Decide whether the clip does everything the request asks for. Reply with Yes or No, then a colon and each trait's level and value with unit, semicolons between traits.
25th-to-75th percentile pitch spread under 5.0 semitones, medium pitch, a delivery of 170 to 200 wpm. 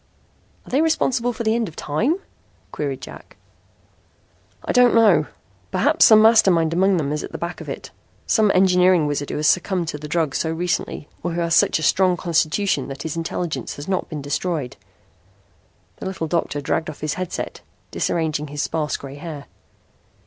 Yes: average, 4.1 semitones; medium, 170 Hz; average, 180 wpm